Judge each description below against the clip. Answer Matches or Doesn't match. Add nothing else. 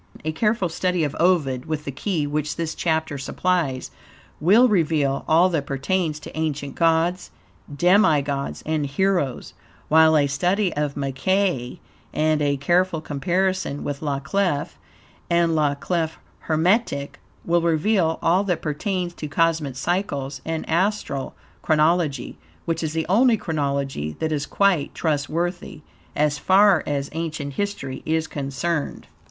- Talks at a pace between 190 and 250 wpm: Doesn't match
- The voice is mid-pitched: Matches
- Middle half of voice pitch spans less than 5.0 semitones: Matches